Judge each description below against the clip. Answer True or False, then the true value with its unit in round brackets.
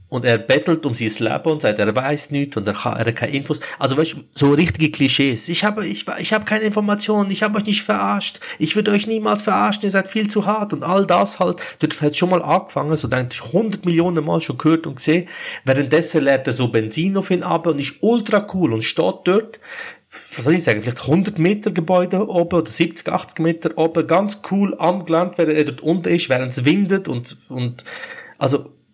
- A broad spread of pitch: True (5.7 semitones)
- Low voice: False (165 Hz)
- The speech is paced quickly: True (220 wpm)